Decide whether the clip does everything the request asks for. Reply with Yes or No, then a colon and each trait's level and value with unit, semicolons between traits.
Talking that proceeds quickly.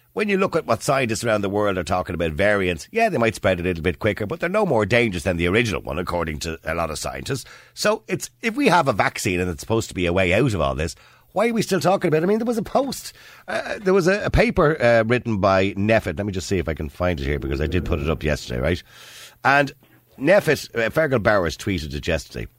Yes: fast, 275 wpm